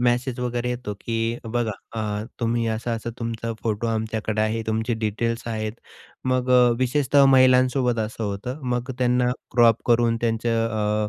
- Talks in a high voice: No, low, 115 Hz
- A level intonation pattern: Yes, narrow, 1.9 semitones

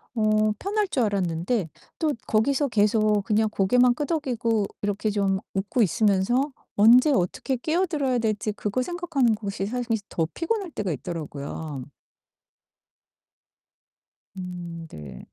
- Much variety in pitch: No, average, 5.0 semitones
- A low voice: No, high, 215 Hz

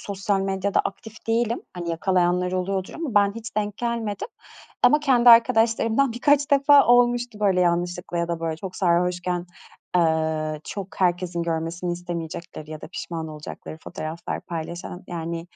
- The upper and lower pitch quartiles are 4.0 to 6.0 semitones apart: Yes, average, 4.8 semitones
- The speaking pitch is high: No, medium, 180 Hz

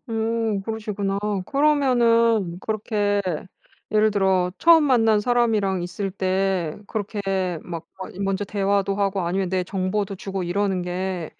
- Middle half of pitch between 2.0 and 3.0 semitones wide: Yes, average, 2.7 semitones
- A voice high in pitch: Yes, high, 200 Hz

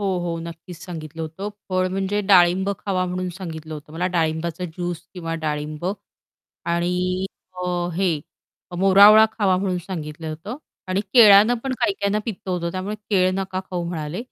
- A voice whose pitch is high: No, medium, 180 Hz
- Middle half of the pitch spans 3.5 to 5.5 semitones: No, average, 2.7 semitones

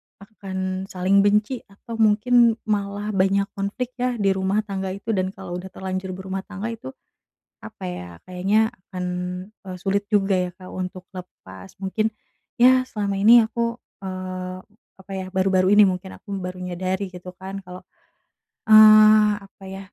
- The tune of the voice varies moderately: No, narrow, 2.2 semitones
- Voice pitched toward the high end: Yes, high, 195 Hz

